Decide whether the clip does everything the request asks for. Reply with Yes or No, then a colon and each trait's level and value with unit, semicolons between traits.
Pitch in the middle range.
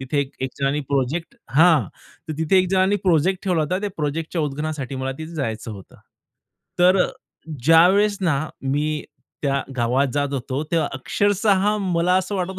Yes: medium, 160 Hz